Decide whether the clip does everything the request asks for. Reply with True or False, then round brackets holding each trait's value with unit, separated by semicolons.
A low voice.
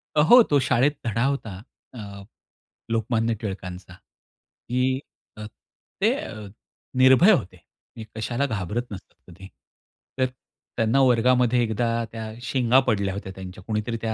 True (115 Hz)